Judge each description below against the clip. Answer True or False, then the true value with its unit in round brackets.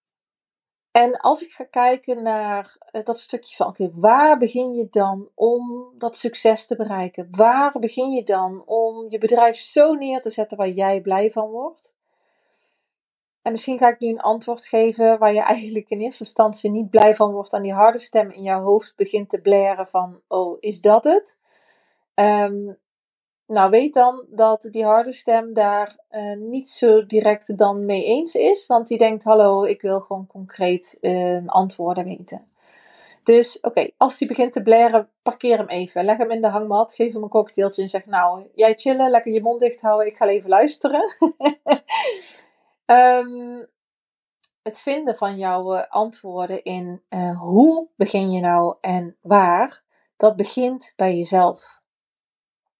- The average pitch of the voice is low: False (220 Hz)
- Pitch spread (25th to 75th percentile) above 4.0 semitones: False (3.4 semitones)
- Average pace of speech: True (170 wpm)